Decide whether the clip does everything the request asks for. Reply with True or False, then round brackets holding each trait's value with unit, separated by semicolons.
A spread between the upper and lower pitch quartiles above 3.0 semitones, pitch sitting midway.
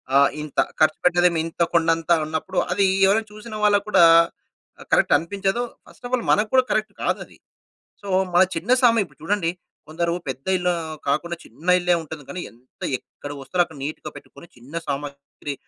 True (4.7 semitones; 170 Hz)